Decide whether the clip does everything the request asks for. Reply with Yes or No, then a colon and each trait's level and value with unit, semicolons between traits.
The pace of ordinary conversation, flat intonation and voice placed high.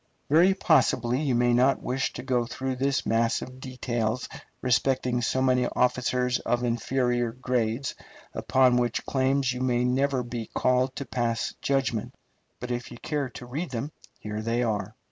No: average, 165 wpm; narrow, 1.5 semitones; low, 125 Hz